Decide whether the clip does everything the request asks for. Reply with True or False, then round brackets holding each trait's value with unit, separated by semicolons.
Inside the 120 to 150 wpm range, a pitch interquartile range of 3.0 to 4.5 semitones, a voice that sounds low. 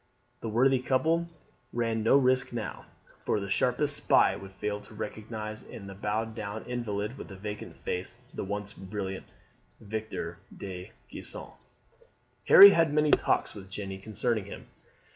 True (145 wpm; 3.6 semitones; 110 Hz)